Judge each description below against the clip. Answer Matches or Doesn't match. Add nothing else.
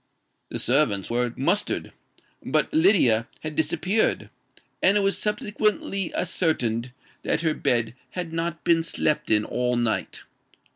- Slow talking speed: Matches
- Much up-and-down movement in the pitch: Matches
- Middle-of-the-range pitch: Matches